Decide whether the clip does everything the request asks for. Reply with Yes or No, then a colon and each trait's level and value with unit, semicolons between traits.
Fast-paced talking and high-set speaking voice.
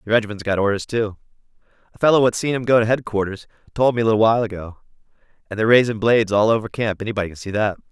No: fast, 220 wpm; low, 110 Hz